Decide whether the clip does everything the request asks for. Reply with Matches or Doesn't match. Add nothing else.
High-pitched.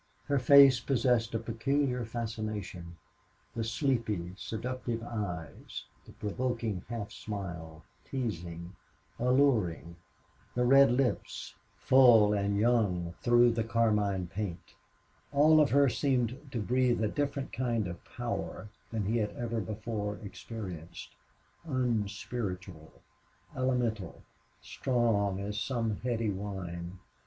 Doesn't match